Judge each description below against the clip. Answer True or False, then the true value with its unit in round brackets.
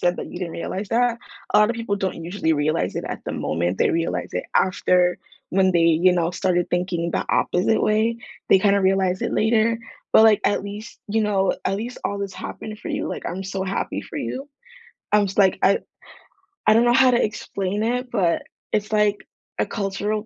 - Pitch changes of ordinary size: True (3.1 semitones)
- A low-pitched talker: False (195 Hz)